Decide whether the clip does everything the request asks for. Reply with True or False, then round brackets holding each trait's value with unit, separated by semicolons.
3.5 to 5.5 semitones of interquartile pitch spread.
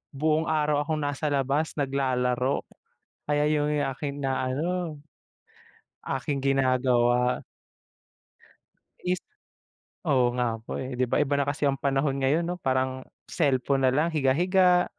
False (2.6 semitones)